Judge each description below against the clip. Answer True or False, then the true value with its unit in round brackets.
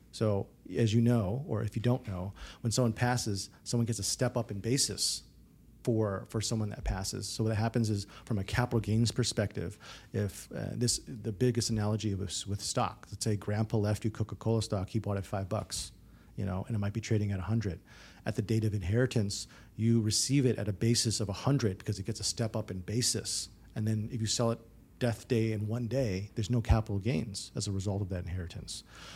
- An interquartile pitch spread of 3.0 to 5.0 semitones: False (2.4 semitones)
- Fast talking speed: True (220 wpm)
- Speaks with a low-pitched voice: True (110 Hz)